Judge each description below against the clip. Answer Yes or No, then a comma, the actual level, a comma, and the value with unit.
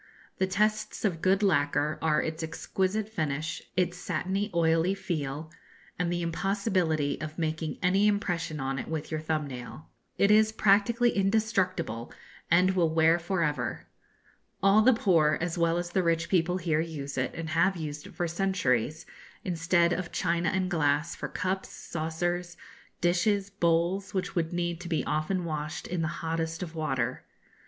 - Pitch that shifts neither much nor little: Yes, average, 3.1 semitones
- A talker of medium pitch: Yes, medium, 170 Hz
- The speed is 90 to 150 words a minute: No, average, 165 wpm